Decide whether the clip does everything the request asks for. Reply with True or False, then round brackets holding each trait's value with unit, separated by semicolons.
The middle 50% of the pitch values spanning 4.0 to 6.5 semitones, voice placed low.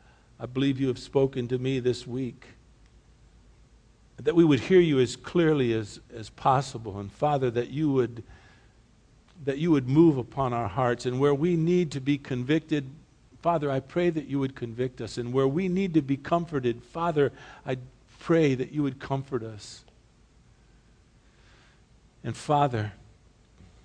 False (3.6 semitones; 130 Hz)